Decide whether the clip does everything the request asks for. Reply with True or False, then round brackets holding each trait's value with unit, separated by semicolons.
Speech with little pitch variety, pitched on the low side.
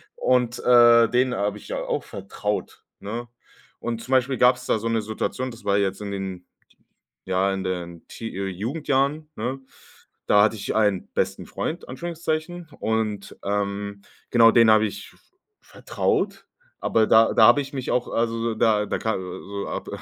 False (3.7 semitones; 110 Hz)